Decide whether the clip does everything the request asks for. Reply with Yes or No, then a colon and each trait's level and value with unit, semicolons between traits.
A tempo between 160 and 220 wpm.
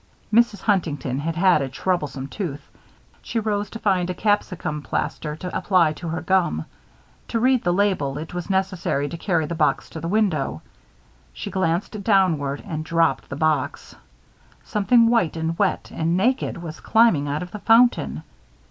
Yes: average, 165 wpm